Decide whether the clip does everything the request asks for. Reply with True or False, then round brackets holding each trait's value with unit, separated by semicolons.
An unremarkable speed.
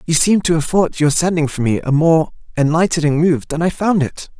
False (230 wpm)